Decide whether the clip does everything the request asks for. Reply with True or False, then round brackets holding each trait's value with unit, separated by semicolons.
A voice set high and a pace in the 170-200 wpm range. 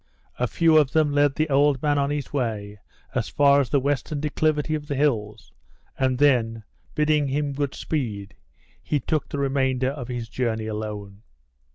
False (140 Hz; 175 wpm)